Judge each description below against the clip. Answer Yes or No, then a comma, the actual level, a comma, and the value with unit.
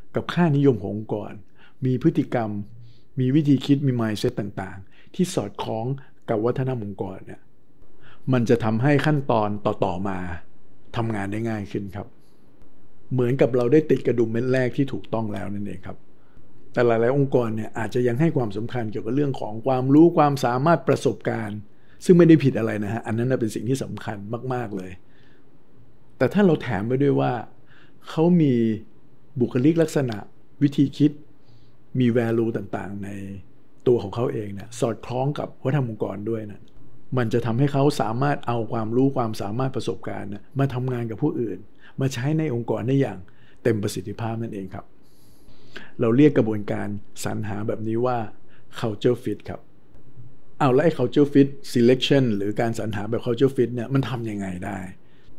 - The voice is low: Yes, low, 120 Hz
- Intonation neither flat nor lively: Yes, average, 4.0 semitones